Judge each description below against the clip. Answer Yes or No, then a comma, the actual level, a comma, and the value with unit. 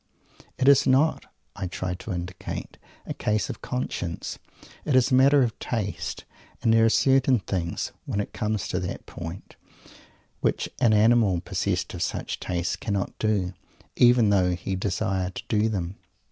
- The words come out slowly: No, average, 160 wpm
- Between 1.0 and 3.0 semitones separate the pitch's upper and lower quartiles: No, average, 4.6 semitones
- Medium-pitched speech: No, low, 105 Hz